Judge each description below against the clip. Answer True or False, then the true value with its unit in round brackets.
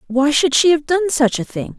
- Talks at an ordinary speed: False (270 wpm)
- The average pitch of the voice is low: False (295 Hz)